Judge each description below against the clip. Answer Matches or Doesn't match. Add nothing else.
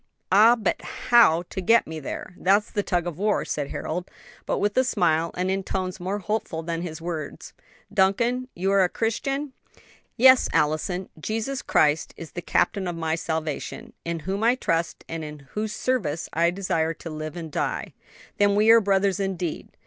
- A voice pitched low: Doesn't match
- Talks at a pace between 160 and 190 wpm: Matches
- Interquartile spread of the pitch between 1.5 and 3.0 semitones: Doesn't match